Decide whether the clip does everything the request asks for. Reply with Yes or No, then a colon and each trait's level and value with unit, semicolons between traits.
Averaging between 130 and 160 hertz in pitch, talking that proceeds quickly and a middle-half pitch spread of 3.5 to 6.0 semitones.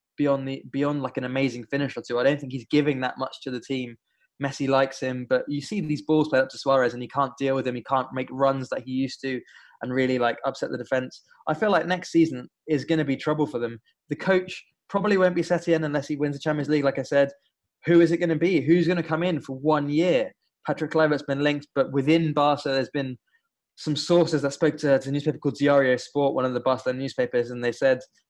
No: medium, 140 Hz; fast, 250 wpm; average, 2.9 semitones